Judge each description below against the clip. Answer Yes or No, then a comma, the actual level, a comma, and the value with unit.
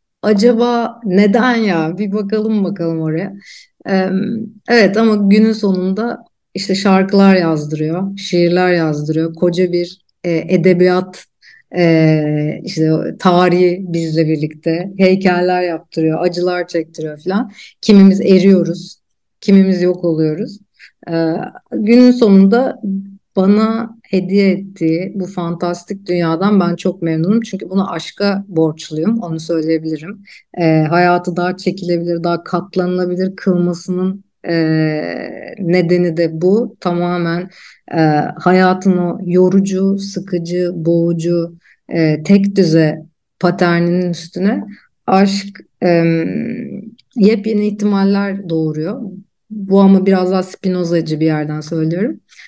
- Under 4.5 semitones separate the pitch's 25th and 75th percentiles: Yes, average, 2.7 semitones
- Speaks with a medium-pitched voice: Yes, medium, 180 Hz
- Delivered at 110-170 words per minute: No, average, 100 wpm